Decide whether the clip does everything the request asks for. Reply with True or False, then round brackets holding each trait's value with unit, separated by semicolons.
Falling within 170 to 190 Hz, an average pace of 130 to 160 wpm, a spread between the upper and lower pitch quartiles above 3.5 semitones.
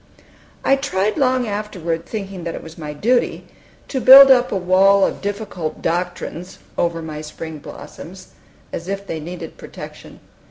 True (185 Hz; 155 wpm; 4.3 semitones)